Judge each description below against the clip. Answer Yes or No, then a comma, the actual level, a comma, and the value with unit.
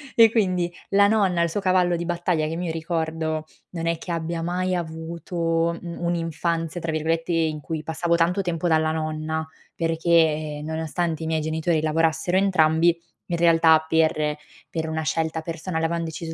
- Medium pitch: Yes, medium, 165 Hz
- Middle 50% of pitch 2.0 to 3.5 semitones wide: No, narrow, 1.4 semitones